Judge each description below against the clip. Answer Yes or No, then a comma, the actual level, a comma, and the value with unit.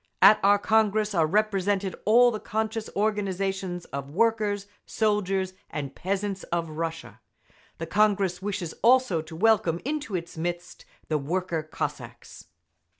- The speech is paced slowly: Yes, slow, 130 wpm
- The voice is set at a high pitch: Yes, high, 195 Hz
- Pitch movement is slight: No, average, 3.9 semitones